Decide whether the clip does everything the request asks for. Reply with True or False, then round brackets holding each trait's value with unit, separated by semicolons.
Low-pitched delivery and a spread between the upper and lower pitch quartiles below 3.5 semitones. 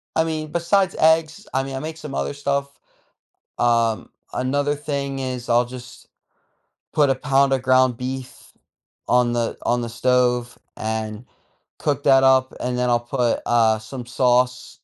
True (130 Hz; 2.6 semitones)